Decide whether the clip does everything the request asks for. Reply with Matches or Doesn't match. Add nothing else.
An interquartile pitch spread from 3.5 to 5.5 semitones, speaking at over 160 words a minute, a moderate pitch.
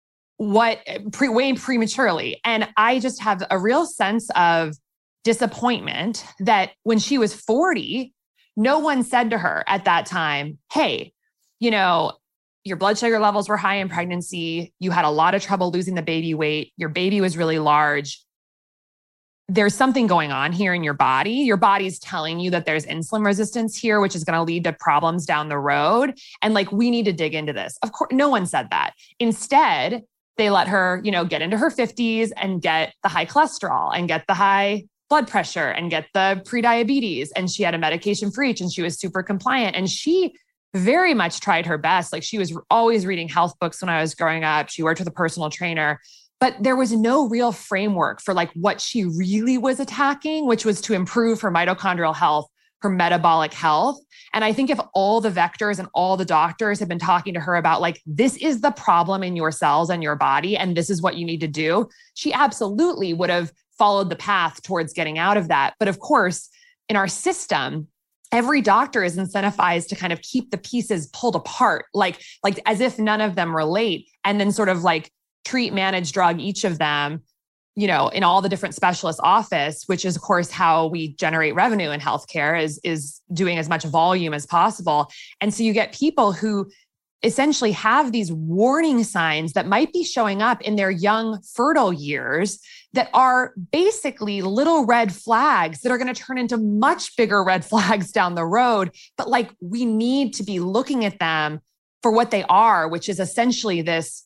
Doesn't match